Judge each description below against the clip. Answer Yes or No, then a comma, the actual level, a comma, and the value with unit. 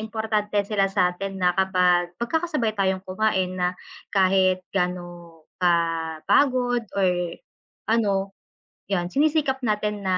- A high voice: Yes, high, 195 Hz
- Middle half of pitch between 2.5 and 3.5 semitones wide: Yes, average, 3.1 semitones